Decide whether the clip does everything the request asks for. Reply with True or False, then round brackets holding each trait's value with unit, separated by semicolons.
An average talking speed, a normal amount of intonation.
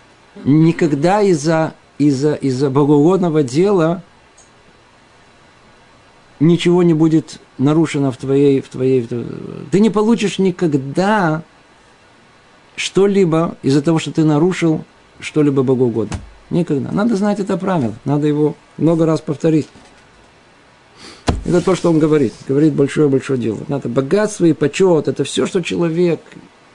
True (120 wpm; 3.8 semitones)